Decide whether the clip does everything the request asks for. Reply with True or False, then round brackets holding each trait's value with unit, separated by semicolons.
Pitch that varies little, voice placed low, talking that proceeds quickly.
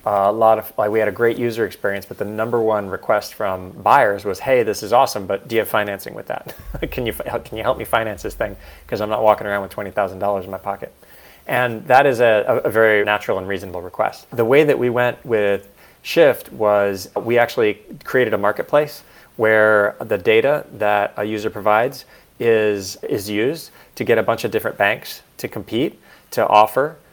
True (1.8 semitones; 105 Hz; 210 wpm)